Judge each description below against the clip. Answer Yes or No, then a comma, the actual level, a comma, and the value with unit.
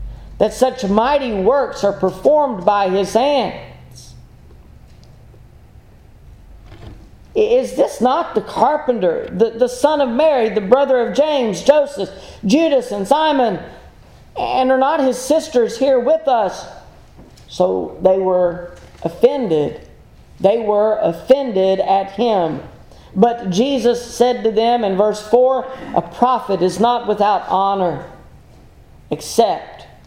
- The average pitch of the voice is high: Yes, high, 225 Hz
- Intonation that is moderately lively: No, wide, 5.7 semitones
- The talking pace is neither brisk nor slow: No, slow, 120 wpm